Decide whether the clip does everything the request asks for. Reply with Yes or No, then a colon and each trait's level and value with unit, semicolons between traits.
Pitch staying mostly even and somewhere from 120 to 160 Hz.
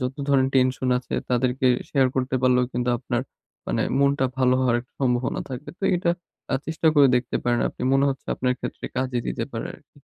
Yes: narrow, 1.3 semitones; low, 130 Hz